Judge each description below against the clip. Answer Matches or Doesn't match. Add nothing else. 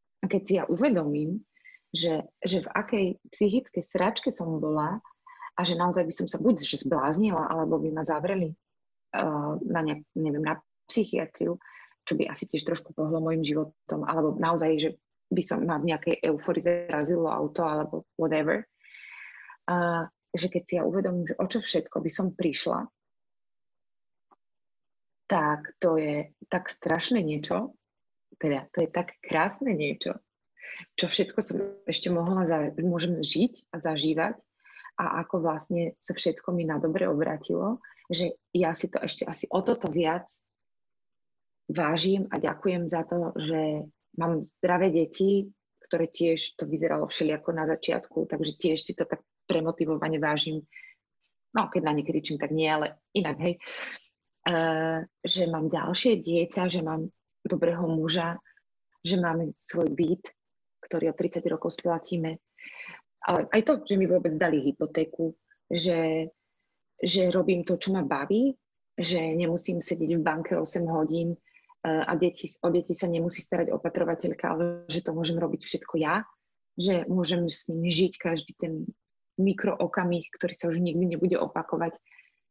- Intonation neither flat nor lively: Doesn't match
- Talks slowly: Doesn't match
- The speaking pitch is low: Doesn't match